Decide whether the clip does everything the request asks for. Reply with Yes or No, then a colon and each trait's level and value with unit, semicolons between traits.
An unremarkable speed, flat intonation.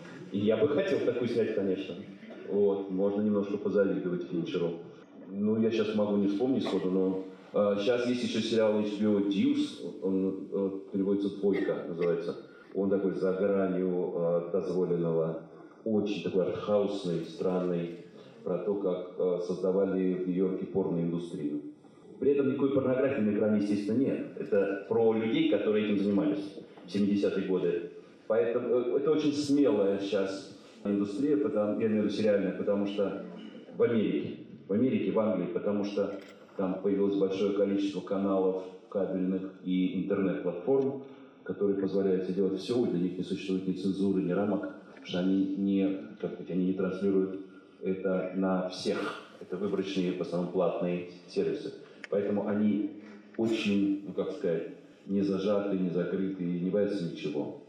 Yes: average, 145 wpm; narrow, 1.7 semitones